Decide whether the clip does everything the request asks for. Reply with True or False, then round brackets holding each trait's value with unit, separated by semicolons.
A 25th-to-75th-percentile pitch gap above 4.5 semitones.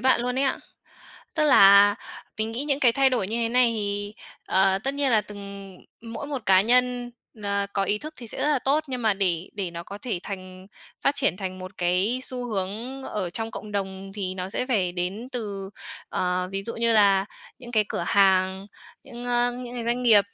False (4.2 semitones)